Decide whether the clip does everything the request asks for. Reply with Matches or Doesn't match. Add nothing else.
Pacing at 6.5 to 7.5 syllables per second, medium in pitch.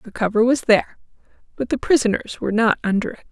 Doesn't match